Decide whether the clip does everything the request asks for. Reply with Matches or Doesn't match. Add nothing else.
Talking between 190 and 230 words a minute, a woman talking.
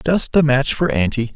Doesn't match